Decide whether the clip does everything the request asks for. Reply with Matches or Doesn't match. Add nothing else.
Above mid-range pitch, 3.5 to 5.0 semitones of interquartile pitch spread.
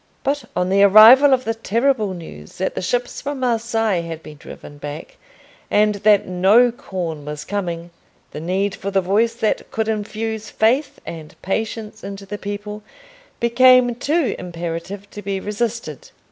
Matches